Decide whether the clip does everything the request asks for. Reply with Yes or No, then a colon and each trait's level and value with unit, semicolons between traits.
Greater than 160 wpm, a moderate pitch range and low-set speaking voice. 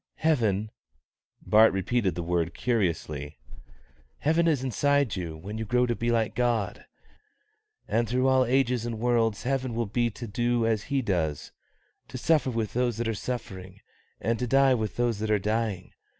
Yes: average, 170 wpm; average, 3.4 semitones; low, 115 Hz